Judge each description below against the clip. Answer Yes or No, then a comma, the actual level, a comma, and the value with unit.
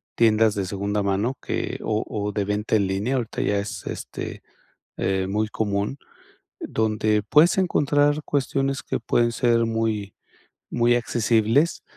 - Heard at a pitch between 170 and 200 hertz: No, low, 110 Hz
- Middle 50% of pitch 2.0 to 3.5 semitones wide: Yes, average, 2.9 semitones